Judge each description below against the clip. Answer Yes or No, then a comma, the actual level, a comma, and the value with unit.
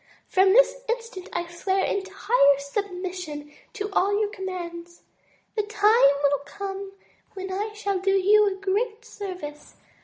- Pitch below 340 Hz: No, very high, 390 Hz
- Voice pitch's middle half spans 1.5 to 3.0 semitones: Yes, narrow, 2.6 semitones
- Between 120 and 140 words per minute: Yes, slow, 135 wpm